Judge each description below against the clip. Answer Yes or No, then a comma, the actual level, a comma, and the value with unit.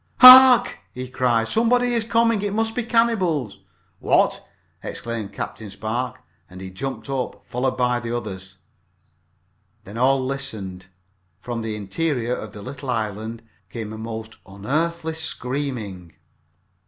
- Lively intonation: Yes, wide, 6.7 semitones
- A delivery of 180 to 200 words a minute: No, slow, 135 wpm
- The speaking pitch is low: Yes, low, 125 Hz